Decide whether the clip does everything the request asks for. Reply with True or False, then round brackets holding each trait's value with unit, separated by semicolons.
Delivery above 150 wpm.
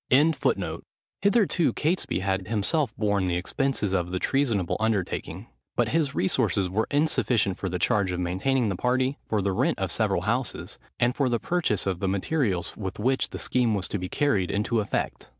True (185 wpm)